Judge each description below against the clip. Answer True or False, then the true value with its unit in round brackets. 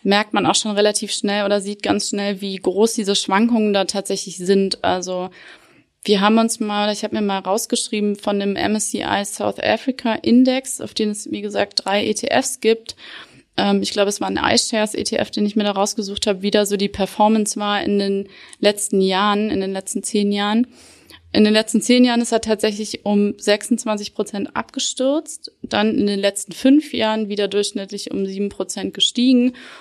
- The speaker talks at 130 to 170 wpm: False (185 wpm)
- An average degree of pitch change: False (2.0 semitones)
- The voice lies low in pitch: False (210 Hz)